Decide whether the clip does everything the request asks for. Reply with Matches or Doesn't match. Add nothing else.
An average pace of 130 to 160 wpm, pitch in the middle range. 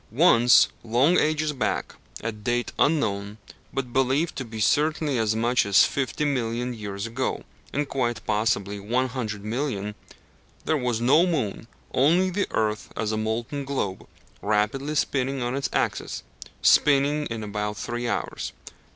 Doesn't match